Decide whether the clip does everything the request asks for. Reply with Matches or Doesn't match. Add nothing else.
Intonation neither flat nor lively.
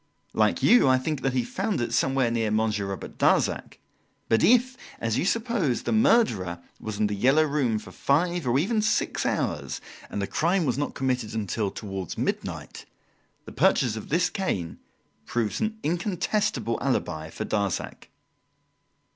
Doesn't match